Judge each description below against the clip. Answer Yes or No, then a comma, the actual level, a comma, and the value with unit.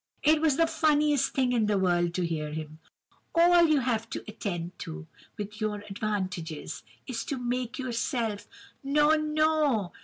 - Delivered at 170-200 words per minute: No, average, 145 wpm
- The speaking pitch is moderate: No, high, 235 Hz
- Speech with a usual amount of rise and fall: No, wide, 7.8 semitones